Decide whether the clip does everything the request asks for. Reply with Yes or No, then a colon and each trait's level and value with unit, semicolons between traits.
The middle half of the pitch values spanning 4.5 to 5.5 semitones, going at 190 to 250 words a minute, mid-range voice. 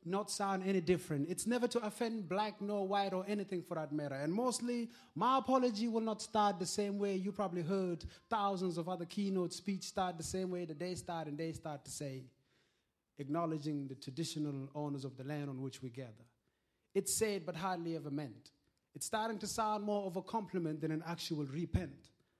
Yes: average, 5.1 semitones; average, 200 wpm; medium, 180 Hz